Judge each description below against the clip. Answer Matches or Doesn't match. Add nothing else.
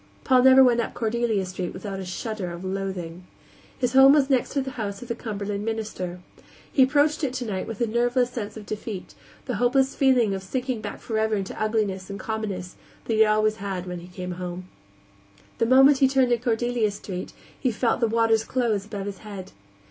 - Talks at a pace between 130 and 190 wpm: Doesn't match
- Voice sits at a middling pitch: Doesn't match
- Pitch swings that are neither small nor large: Matches